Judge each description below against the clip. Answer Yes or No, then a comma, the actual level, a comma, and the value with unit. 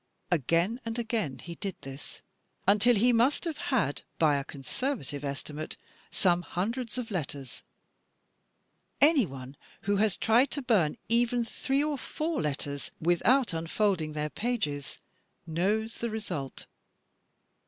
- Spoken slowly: Yes, slow, 130 wpm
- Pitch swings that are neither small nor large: No, wide, 7.9 semitones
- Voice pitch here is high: Yes, high, 200 Hz